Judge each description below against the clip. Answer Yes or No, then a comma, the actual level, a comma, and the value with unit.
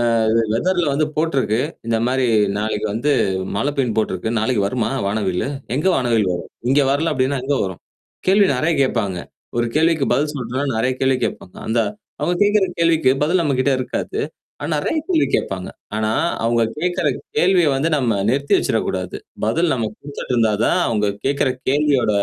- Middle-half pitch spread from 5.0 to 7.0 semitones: Yes, wide, 5.6 semitones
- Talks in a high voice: No, low, 130 Hz